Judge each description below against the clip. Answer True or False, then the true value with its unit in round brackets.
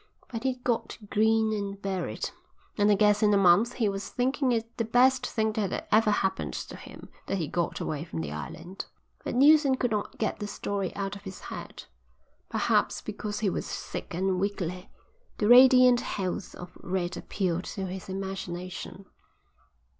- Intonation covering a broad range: False (3.4 semitones)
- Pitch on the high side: True (205 Hz)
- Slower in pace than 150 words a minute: False (185 wpm)